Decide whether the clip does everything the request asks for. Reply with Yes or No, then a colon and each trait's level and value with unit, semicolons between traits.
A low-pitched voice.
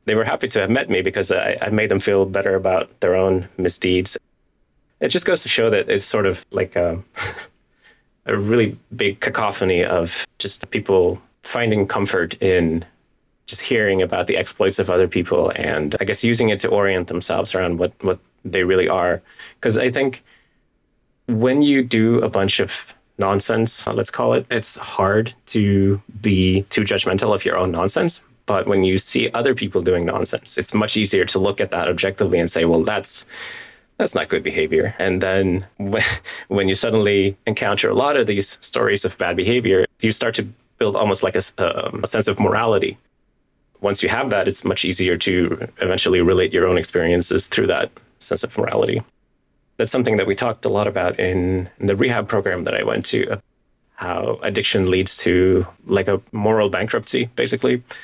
Yes: very low, 95 Hz